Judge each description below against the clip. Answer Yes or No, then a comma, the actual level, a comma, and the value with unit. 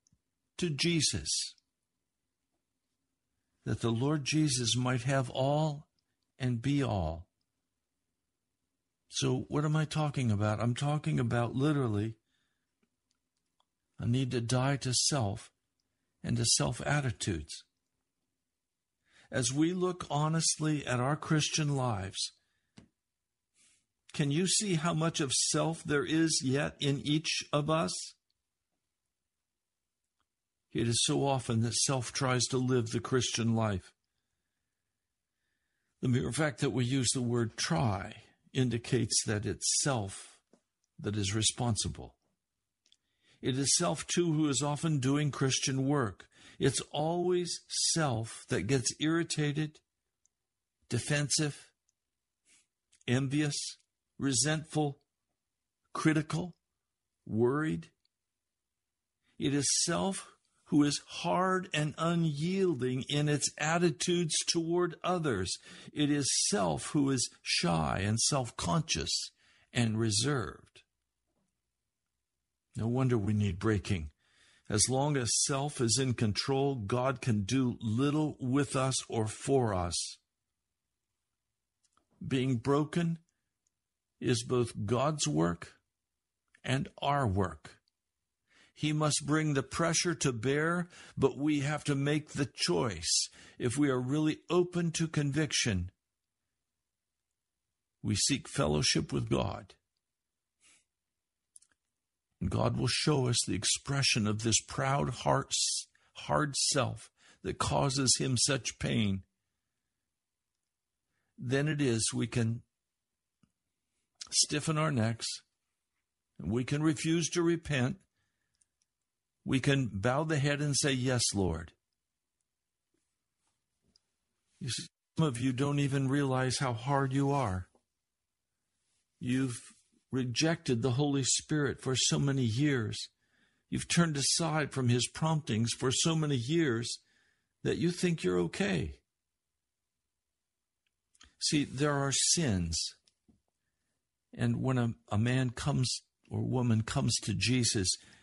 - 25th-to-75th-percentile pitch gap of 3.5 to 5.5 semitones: Yes, average, 4.8 semitones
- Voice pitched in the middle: No, low, 130 Hz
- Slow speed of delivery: Yes, slow, 110 wpm